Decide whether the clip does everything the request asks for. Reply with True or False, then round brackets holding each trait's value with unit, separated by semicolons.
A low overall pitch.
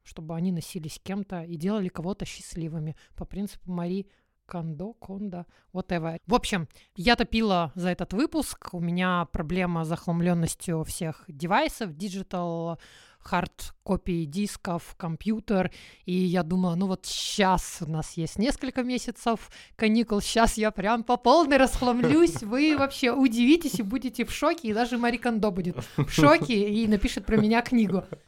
False (195 Hz)